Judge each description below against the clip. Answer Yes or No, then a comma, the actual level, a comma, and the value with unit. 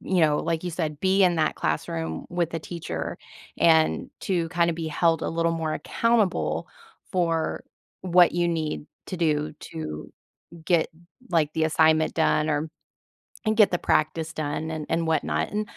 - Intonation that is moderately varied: No, narrow, 2.0 semitones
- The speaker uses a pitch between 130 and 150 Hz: No, medium, 160 Hz